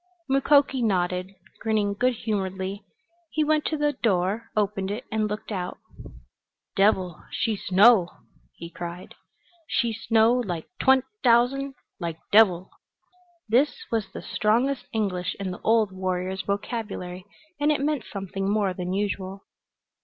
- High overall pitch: Yes, high, 210 Hz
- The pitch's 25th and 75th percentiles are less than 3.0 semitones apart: No, average, 4.1 semitones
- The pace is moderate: No, slow, 130 wpm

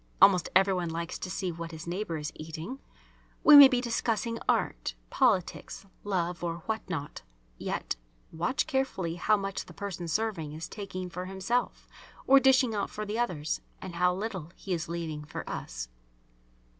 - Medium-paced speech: Yes, average, 170 wpm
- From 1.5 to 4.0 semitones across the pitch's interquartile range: No, average, 4.6 semitones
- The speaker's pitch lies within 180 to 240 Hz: Yes, medium, 185 Hz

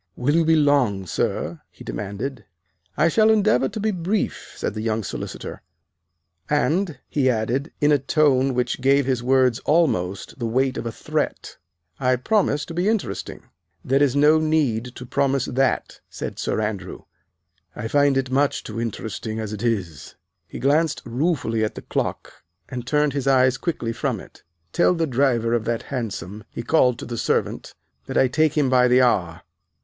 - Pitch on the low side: Yes, low, 130 Hz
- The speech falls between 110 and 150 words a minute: No, average, 175 wpm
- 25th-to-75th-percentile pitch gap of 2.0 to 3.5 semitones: No, average, 4.4 semitones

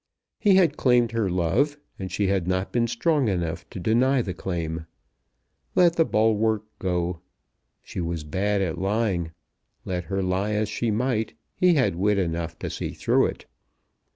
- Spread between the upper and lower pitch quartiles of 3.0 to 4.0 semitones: No, average, 4.8 semitones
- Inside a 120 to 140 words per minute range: No, average, 165 wpm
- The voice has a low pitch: Yes, low, 100 Hz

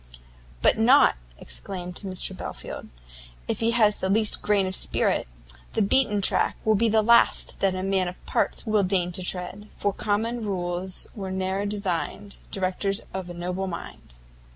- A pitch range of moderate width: No, narrow, 2.2 semitones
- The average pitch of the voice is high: Yes, high, 195 Hz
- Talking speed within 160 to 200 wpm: Yes, average, 165 wpm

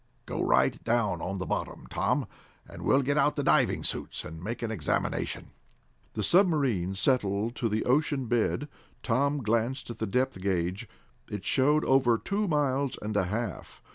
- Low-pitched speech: Yes, low, 120 Hz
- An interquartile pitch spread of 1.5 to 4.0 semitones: No, average, 5.2 semitones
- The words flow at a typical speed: Yes, average, 170 wpm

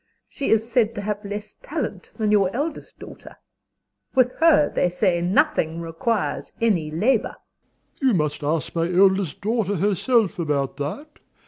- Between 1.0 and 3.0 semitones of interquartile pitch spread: No, wide, 5.5 semitones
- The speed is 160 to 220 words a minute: No, average, 150 wpm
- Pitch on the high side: Yes, high, 205 Hz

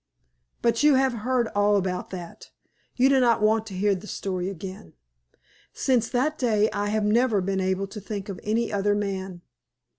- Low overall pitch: No, high, 210 Hz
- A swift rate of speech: No, average, 180 wpm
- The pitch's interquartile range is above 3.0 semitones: Yes, average, 3.4 semitones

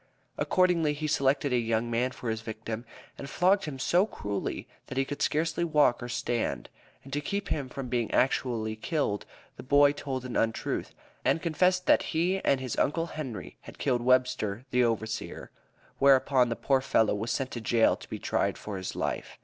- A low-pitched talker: Yes, low, 130 Hz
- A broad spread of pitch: No, average, 4.2 semitones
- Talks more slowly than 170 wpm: No, average, 185 wpm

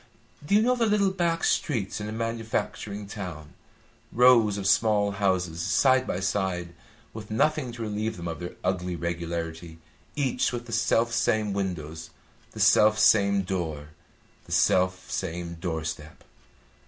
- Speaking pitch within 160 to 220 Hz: No, low, 100 Hz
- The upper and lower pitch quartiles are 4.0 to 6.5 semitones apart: Yes, average, 4.8 semitones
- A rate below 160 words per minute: Yes, average, 150 wpm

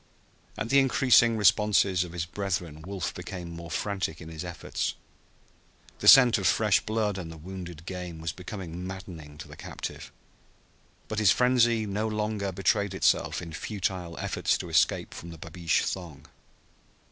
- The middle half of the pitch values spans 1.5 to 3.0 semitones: No, average, 3.9 semitones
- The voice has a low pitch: Yes, very low, 95 Hz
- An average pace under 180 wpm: Yes, average, 160 wpm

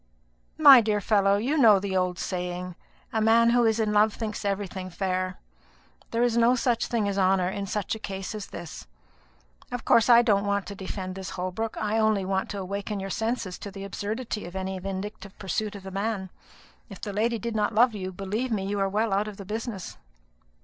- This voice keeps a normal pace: No, fast, 210 wpm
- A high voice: Yes, high, 205 Hz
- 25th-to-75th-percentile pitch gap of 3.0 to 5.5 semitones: No, narrow, 2.5 semitones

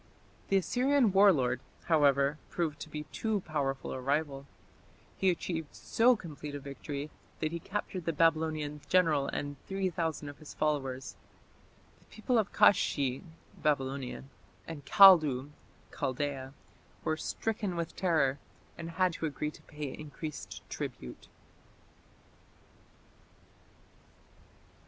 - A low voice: No, medium, 155 Hz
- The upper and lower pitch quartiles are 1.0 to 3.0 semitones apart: No, average, 4.0 semitones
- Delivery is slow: Yes, slow, 120 wpm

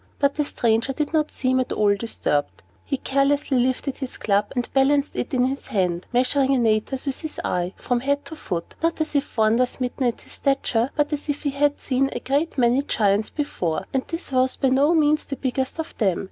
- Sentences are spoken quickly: Yes, fast, 215 wpm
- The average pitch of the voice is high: Yes, very high, 265 Hz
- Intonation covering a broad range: No, average, 3.5 semitones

